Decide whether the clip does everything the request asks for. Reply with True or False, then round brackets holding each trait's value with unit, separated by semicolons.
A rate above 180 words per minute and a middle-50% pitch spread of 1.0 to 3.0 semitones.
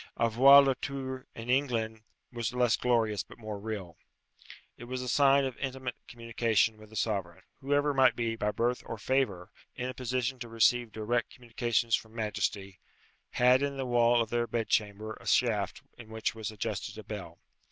False (175 wpm; 2.7 semitones)